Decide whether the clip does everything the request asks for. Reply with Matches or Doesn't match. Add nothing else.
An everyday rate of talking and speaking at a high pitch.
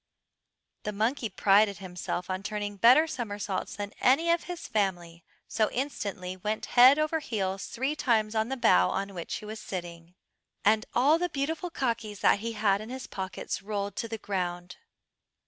Matches